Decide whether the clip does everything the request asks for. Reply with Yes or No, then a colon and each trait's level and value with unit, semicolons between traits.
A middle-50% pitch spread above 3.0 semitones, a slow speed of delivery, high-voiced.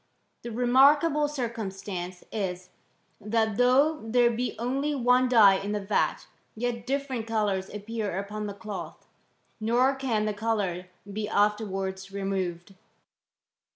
Yes: average, 3.9 semitones; slow, 125 wpm; high, 220 Hz